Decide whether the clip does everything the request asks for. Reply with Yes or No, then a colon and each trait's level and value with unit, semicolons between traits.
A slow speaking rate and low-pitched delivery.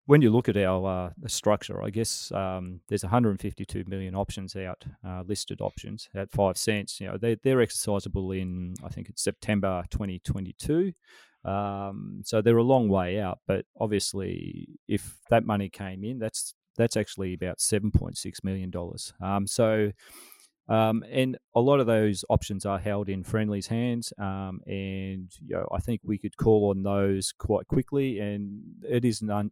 No: average, 170 wpm; low, 105 Hz